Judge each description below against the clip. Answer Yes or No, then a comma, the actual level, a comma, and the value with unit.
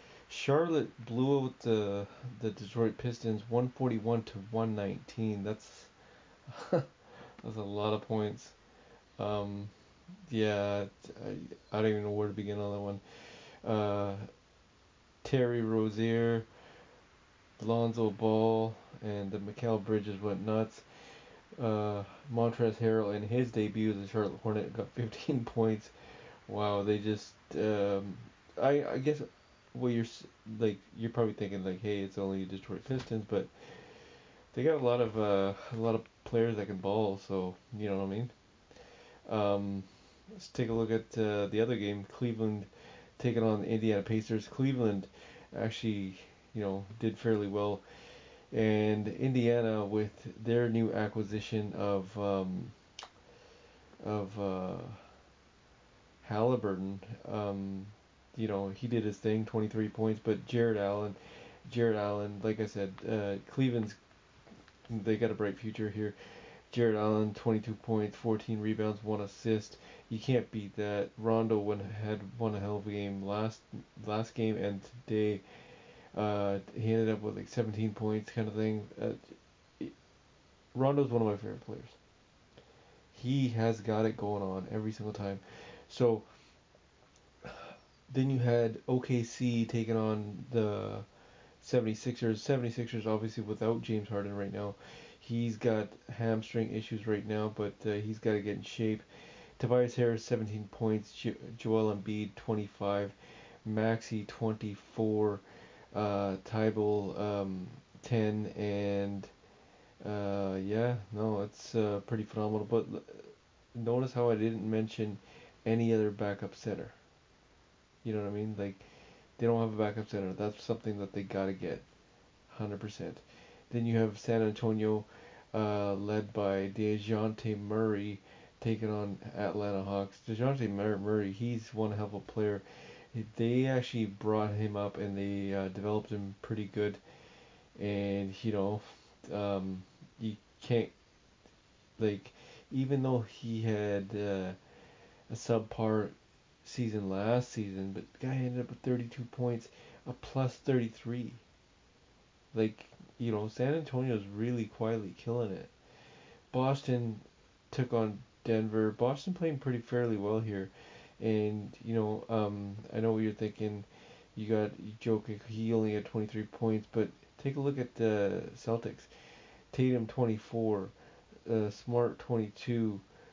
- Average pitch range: No, narrow, 2.1 semitones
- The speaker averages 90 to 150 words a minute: Yes, slow, 135 wpm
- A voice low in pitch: Yes, low, 110 Hz